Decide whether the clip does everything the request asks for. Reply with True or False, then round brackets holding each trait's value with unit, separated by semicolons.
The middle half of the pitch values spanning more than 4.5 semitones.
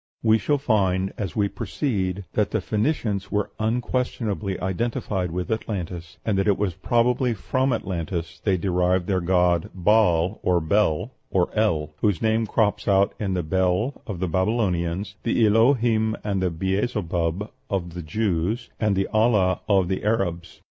False (3.5 semitones)